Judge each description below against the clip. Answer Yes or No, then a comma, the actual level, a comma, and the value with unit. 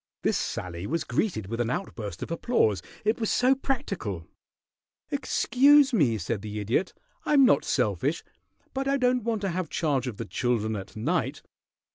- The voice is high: No, medium, 160 Hz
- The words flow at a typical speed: Yes, average, 165 wpm